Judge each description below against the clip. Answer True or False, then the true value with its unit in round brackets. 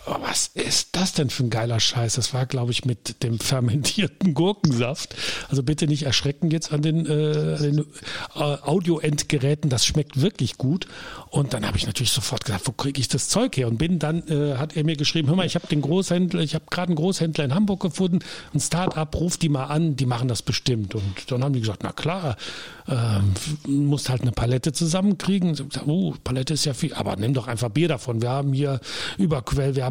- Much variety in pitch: False (4.2 semitones)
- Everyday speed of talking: False (215 wpm)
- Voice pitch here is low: False (145 Hz)